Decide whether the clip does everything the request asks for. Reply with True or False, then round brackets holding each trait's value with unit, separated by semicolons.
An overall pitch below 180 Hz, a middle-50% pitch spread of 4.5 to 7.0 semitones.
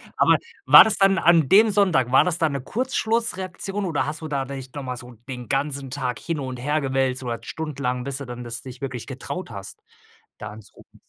True (140 Hz; 5.2 semitones)